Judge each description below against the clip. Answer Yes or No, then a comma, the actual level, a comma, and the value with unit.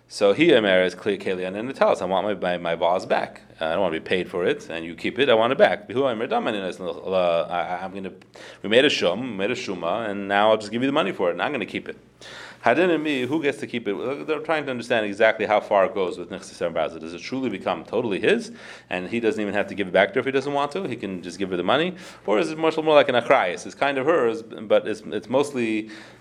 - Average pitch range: No, wide, 6.4 semitones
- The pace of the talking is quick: Yes, fast, 285 wpm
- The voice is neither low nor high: No, low, 105 Hz